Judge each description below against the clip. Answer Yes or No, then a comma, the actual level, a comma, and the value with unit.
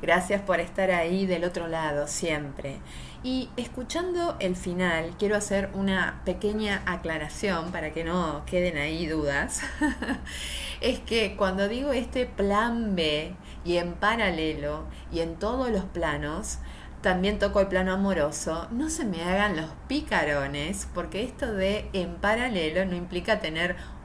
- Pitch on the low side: No, medium, 185 Hz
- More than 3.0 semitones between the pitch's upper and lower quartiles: Yes, average, 4.1 semitones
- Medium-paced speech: Yes, average, 140 wpm